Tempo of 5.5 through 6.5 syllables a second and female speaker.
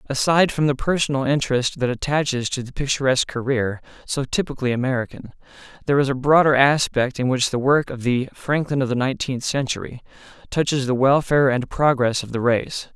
No: 5.9 syllables/s; male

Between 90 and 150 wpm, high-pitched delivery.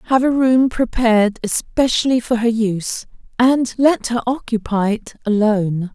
Yes: average, 140 wpm; high, 230 Hz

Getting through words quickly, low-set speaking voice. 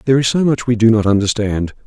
Yes: fast, 260 wpm; low, 115 Hz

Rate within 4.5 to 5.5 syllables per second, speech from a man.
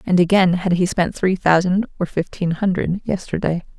No: 5.0 syllables/s; female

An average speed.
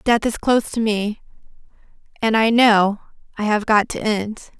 Yes: average, 170 wpm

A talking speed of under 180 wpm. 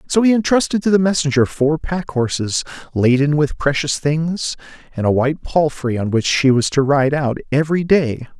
No: average, 185 wpm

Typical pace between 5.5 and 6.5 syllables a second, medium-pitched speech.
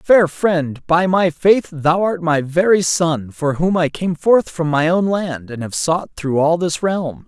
No: 3.8 syllables/s; medium, 170 Hz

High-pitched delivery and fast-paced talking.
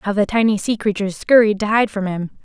Yes: high, 205 Hz; fast, 245 wpm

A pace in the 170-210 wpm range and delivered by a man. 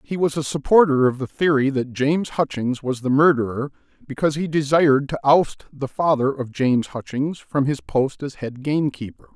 Yes: average, 185 wpm; male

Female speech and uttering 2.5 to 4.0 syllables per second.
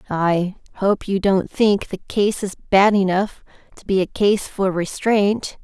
Yes: female; 3.8 syllables/s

